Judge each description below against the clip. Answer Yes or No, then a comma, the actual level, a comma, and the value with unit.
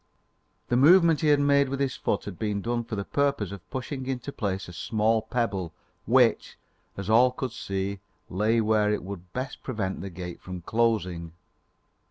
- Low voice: Yes, low, 110 Hz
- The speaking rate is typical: Yes, average, 180 wpm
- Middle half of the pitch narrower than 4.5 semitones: No, average, 4.9 semitones